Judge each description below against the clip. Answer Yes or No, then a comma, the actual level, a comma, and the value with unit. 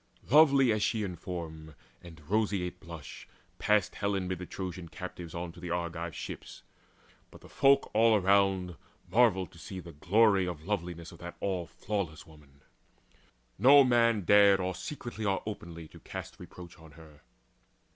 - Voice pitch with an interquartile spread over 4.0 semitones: No, average, 3.7 semitones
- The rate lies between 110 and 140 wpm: No, average, 160 wpm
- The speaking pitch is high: No, very low, 90 Hz